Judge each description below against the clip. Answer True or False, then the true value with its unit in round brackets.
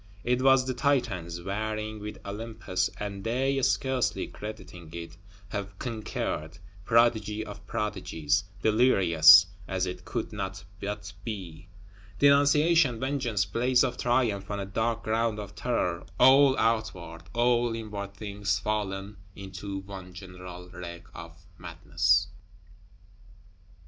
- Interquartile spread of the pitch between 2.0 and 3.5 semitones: False (4.1 semitones)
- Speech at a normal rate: False (120 wpm)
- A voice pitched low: True (105 Hz)